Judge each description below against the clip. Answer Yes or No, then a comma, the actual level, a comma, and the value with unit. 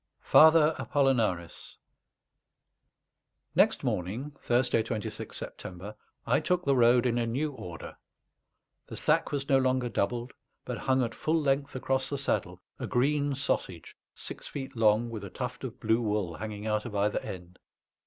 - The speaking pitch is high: No, low, 120 Hz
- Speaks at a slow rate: No, average, 155 wpm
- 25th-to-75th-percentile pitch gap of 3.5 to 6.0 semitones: Yes, average, 4.2 semitones